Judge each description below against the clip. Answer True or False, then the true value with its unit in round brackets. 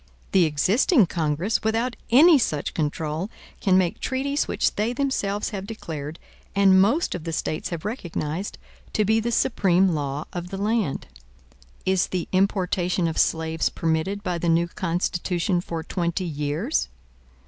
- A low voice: False (185 Hz)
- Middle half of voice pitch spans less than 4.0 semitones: False (4.4 semitones)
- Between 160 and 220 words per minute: False (150 wpm)